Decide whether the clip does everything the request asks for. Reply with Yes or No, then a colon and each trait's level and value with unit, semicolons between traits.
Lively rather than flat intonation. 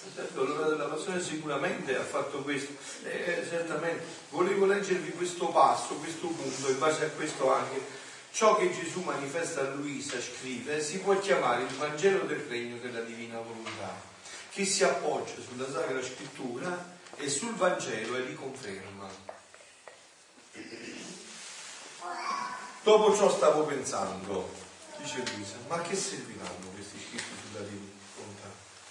Yes: wide, 6.8 semitones